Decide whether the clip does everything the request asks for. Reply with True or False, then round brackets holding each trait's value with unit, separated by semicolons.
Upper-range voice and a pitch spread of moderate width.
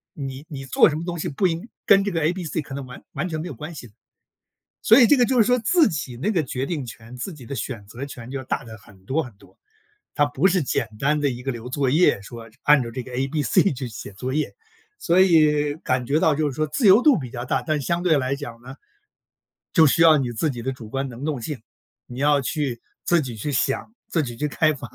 False (140 Hz; 4.3 semitones)